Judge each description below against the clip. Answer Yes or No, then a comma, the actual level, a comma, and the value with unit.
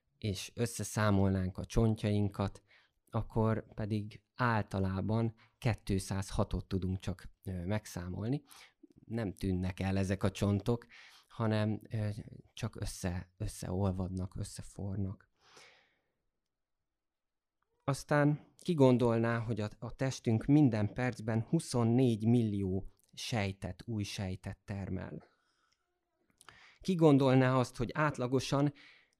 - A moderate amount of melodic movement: Yes, average, 3.6 semitones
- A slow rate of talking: Yes, slow, 80 wpm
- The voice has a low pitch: Yes, low, 105 Hz